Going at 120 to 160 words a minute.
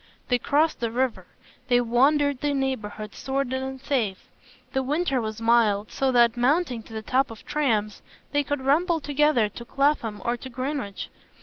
No: average, 170 wpm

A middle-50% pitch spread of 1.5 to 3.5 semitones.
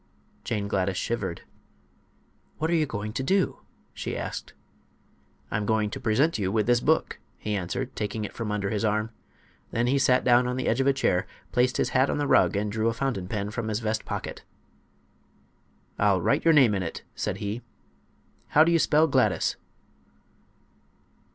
No: average, 4.2 semitones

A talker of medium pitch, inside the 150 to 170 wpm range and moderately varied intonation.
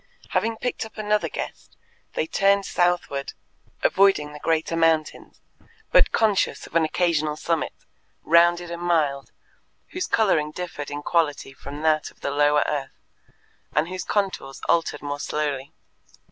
No: medium, 160 Hz; average, 140 wpm; average, 3.3 semitones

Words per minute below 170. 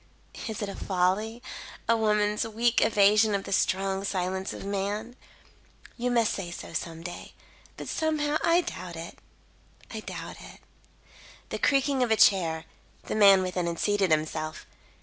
Yes: average, 155 wpm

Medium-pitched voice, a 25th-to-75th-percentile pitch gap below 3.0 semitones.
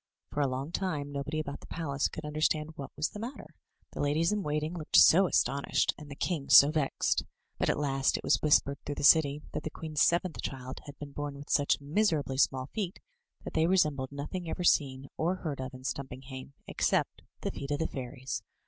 Yes: medium, 145 Hz; narrow, 2.5 semitones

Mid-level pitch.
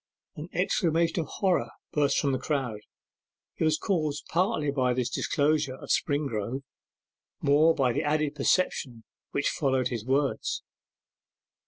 Yes: medium, 145 Hz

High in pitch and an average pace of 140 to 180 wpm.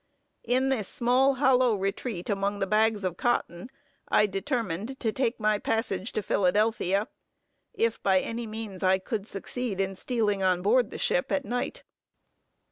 Yes: high, 215 Hz; average, 155 wpm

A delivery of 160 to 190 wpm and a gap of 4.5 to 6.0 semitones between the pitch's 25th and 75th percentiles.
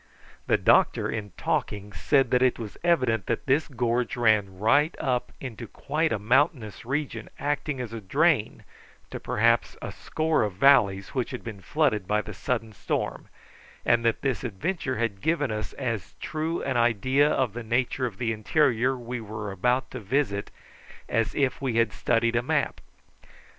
No: average, 170 wpm; average, 3.9 semitones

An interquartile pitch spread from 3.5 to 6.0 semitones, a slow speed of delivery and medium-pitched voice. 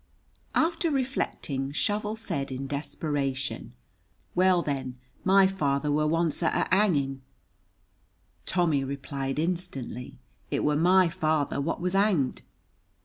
Yes: average, 5.2 semitones; slow, 115 wpm; medium, 150 Hz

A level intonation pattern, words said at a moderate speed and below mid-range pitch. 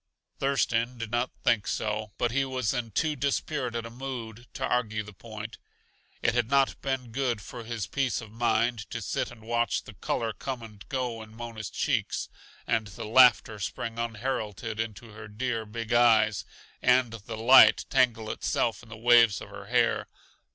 Yes: narrow, 2.2 semitones; average, 175 wpm; low, 115 Hz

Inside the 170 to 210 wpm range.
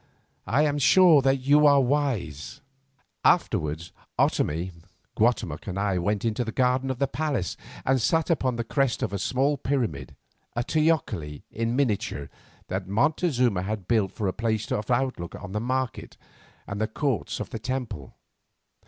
No: average, 160 wpm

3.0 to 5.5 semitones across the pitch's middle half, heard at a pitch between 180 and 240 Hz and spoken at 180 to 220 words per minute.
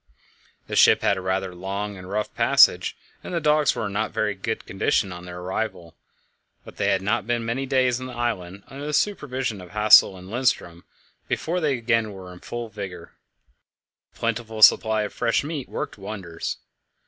No: average, 4.3 semitones; low, 105 Hz; average, 190 wpm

